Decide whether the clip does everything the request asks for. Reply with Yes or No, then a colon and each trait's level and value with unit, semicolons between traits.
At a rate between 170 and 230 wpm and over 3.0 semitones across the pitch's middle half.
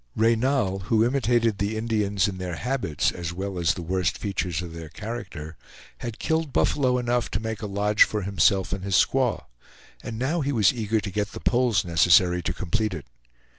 Yes: average, 190 wpm; average, 4.4 semitones